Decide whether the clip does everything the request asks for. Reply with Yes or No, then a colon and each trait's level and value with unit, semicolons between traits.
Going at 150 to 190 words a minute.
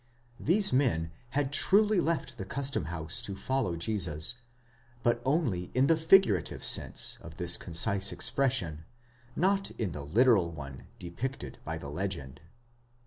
No: average, 140 wpm